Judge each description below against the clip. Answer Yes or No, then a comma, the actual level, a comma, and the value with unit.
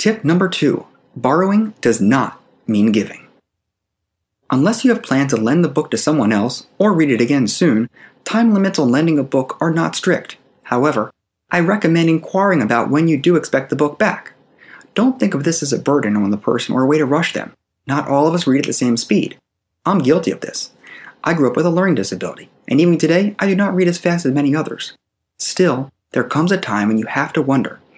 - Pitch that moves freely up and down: Yes, wide, 5.8 semitones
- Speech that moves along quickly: Yes, fast, 220 wpm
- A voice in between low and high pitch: Yes, medium, 155 Hz